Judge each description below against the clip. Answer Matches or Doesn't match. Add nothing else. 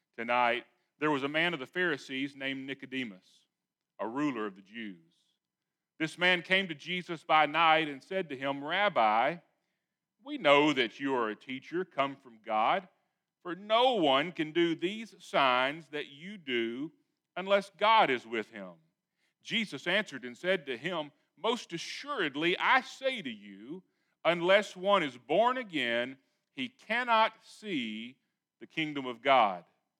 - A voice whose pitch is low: Doesn't match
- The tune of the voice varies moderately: Doesn't match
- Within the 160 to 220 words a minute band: Doesn't match